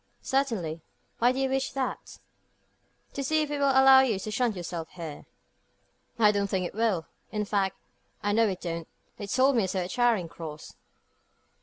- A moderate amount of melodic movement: No, wide, 6.5 semitones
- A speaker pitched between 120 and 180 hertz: No, high, 210 Hz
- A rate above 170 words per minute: Yes, average, 180 wpm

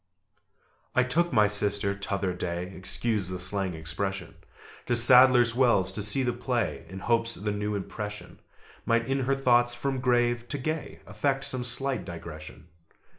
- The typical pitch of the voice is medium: No, low, 115 Hz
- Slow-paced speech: No, average, 155 wpm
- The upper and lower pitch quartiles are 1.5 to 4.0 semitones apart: No, average, 4.4 semitones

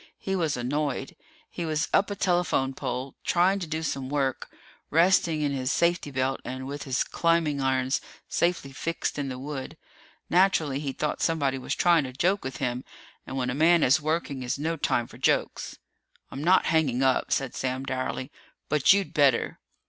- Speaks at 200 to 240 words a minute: No, average, 180 wpm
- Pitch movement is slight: No, average, 4.0 semitones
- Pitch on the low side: No, medium, 145 Hz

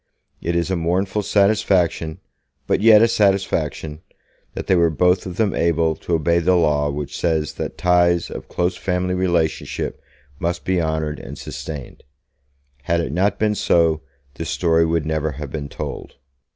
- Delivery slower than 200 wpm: Yes, average, 165 wpm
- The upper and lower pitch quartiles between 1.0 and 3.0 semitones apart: Yes, average, 2.7 semitones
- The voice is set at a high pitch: No, very low, 85 Hz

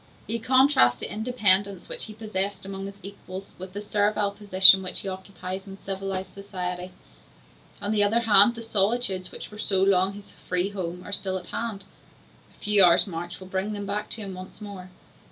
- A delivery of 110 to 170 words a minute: No, average, 190 wpm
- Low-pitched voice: No, high, 195 Hz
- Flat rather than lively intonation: Yes, narrow, 1.8 semitones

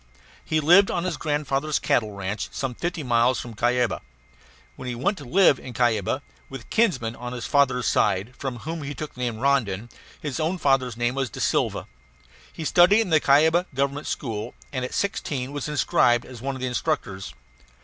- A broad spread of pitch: No, average, 4.2 semitones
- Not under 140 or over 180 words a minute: No, average, 190 wpm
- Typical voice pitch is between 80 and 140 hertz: Yes, low, 135 Hz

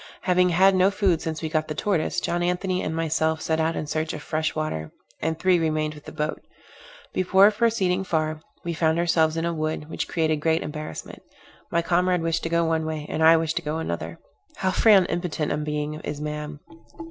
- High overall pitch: No, medium, 160 Hz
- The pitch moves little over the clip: Yes, narrow, 2.2 semitones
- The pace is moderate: No, fast, 210 wpm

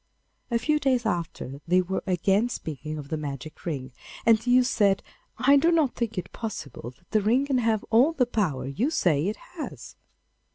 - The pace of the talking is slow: No, average, 195 wpm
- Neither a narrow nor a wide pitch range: No, wide, 7.8 semitones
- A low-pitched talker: No, high, 210 Hz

